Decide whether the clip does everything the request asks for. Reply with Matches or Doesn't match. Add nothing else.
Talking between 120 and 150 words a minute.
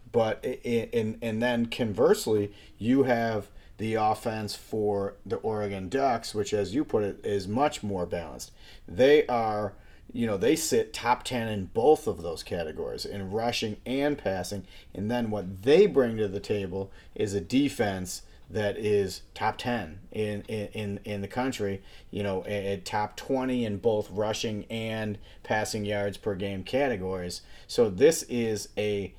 Doesn't match